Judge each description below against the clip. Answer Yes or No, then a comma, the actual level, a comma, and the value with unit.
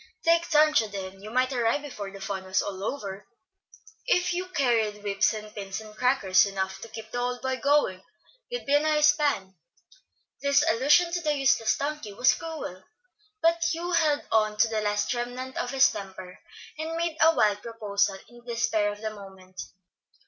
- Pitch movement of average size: No, wide, 6.3 semitones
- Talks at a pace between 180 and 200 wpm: Yes, average, 185 wpm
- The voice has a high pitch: Yes, high, 230 Hz